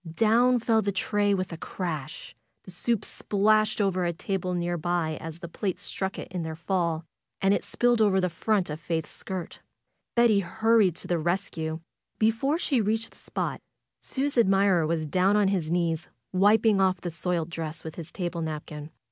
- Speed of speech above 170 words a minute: Yes, average, 180 wpm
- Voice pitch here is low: No, medium, 185 Hz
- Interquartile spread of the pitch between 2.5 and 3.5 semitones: No, average, 3.9 semitones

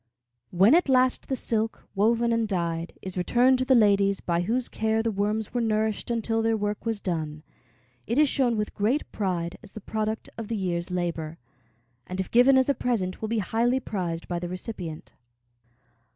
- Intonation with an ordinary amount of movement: Yes, average, 4.2 semitones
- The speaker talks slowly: No, average, 190 wpm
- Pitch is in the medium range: No, high, 215 Hz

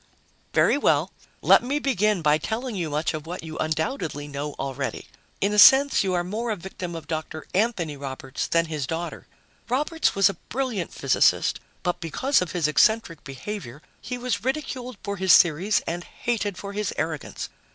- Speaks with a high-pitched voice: No, medium, 180 Hz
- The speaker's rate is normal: Yes, average, 175 wpm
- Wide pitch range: Yes, wide, 5.9 semitones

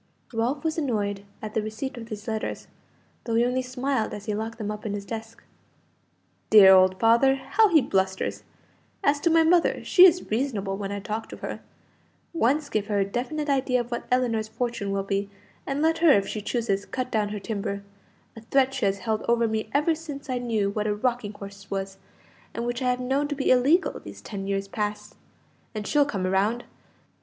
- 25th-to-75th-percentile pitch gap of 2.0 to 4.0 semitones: No, average, 4.5 semitones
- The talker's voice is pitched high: Yes, high, 225 Hz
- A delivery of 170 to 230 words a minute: Yes, fast, 205 wpm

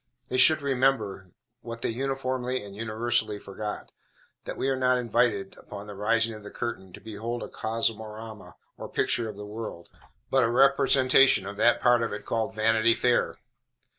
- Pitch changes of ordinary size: Yes, average, 3.2 semitones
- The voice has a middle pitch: No, low, 115 Hz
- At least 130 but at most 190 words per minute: Yes, average, 170 wpm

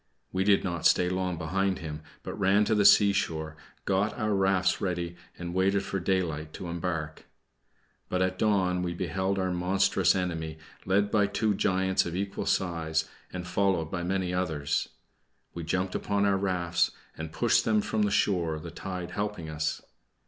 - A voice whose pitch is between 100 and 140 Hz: No, very low, 90 Hz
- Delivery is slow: No, average, 170 wpm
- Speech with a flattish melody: Yes, narrow, 2.3 semitones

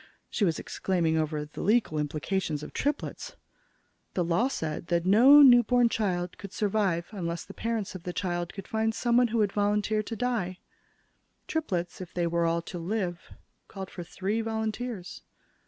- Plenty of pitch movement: No, average, 4.6 semitones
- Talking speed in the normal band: Yes, average, 165 wpm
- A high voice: Yes, high, 195 Hz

